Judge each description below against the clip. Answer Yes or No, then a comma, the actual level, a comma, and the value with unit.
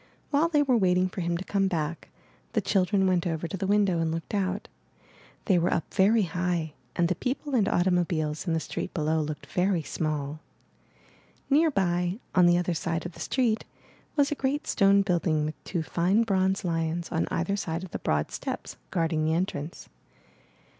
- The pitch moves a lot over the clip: No, average, 3.2 semitones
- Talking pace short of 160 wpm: No, average, 190 wpm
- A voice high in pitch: No, medium, 180 Hz